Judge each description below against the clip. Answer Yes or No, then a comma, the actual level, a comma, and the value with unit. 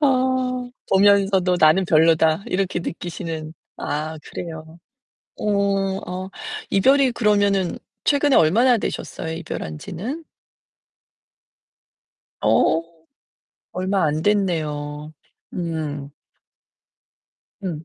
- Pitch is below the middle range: No, medium, 185 Hz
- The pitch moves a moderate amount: Yes, average, 4.3 semitones